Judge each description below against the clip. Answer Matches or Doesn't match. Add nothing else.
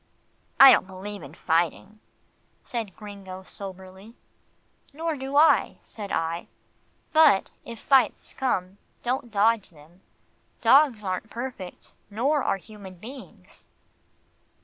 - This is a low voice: Doesn't match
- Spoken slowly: Matches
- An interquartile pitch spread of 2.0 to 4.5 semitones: Doesn't match